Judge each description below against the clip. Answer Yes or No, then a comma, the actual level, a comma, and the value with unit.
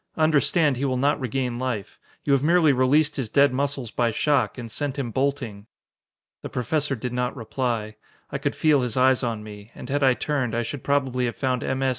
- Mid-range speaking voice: No, low, 130 Hz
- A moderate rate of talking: No, fast, 210 wpm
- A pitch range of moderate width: Yes, average, 3.0 semitones